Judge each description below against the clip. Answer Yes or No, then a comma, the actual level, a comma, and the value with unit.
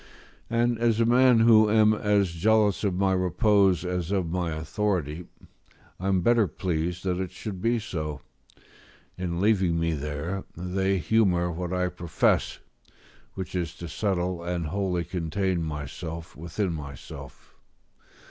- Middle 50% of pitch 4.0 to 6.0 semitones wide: No, average, 3.5 semitones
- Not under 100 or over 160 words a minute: Yes, average, 140 wpm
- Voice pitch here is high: No, very low, 90 Hz